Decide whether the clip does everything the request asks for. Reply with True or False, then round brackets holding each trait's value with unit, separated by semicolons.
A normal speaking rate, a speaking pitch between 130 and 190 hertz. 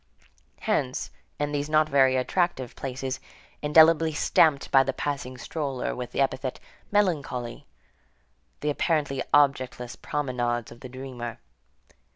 False (120 wpm; 135 Hz)